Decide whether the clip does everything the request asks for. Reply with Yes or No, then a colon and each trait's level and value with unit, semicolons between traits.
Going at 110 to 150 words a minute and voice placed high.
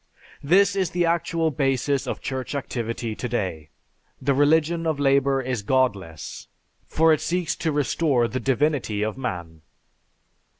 No: average, 140 wpm; low, 135 Hz